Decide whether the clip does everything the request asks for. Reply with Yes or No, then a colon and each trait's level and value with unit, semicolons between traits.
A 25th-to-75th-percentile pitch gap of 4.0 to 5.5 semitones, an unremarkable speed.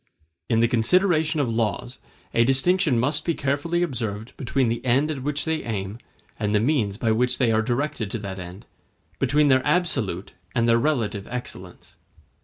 Yes: average, 4.9 semitones; average, 175 wpm